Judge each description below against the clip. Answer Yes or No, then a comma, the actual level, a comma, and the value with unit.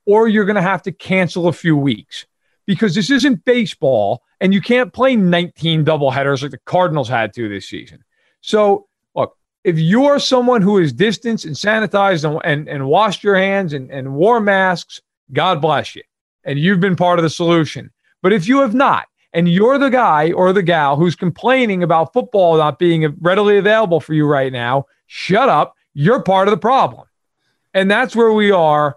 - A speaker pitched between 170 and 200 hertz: Yes, medium, 185 Hz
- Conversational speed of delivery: Yes, average, 195 wpm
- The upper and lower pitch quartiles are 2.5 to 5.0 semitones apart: No, wide, 5.5 semitones